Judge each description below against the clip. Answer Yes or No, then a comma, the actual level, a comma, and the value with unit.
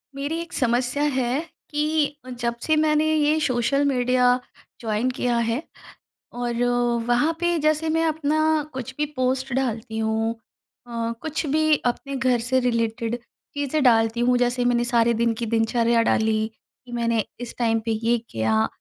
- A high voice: Yes, high, 245 Hz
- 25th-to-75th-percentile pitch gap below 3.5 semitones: No, average, 3.8 semitones